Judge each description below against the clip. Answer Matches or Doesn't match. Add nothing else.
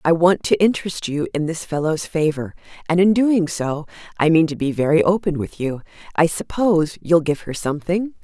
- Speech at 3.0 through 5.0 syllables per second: Doesn't match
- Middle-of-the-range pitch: Matches